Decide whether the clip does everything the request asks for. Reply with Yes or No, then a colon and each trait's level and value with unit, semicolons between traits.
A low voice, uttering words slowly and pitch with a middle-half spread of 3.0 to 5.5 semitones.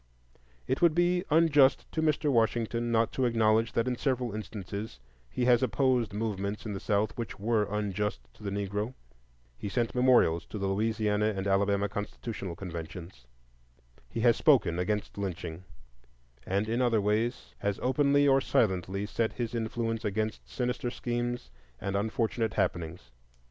No: low, 110 Hz; average, 150 wpm; average, 3.4 semitones